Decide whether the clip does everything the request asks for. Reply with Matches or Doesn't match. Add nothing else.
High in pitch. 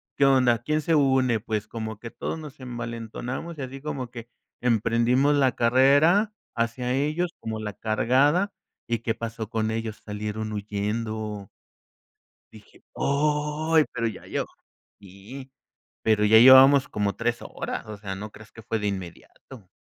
Doesn't match